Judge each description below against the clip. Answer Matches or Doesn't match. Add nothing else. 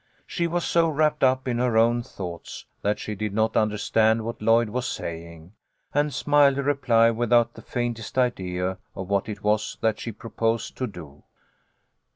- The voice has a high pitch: Doesn't match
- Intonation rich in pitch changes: Doesn't match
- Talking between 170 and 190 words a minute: Matches